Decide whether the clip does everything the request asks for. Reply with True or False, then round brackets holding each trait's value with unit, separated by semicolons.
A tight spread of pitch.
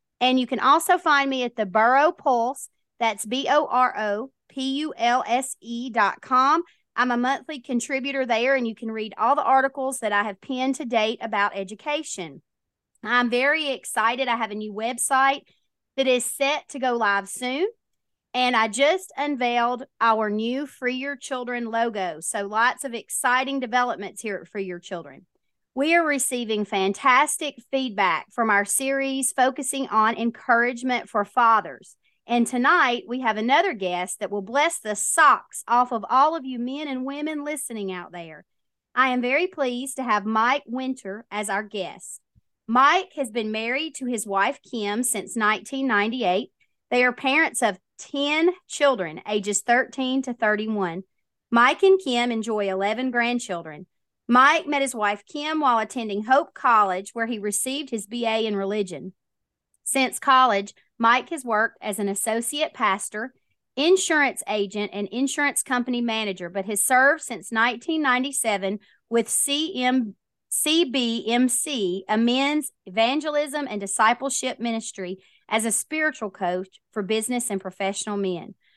False (4.2 semitones)